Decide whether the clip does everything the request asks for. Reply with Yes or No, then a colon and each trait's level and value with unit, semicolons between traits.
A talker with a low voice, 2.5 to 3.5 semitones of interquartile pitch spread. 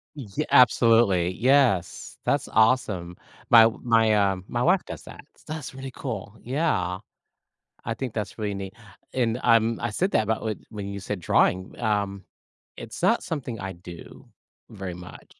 No: low, 110 Hz; average, 4.0 semitones